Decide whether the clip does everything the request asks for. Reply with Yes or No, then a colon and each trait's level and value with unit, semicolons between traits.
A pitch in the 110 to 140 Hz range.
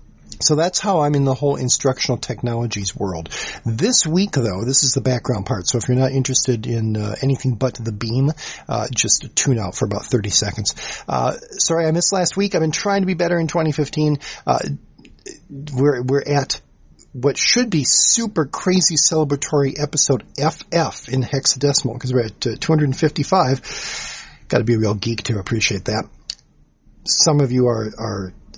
Yes: low, 135 Hz